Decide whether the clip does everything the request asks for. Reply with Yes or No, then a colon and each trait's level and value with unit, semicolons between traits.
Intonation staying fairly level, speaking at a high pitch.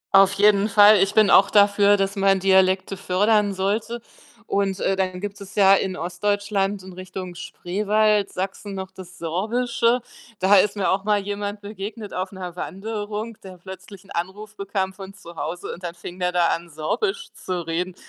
Yes: narrow, 1.9 semitones; high, 195 Hz